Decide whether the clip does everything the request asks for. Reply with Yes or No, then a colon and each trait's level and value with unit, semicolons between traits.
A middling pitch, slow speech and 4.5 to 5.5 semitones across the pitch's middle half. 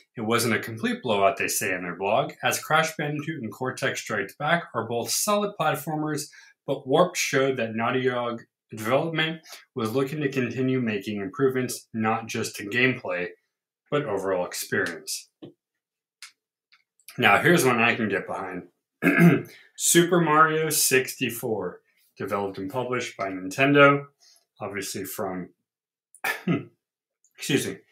No: low, 130 Hz; slow, 130 wpm; average, 5.0 semitones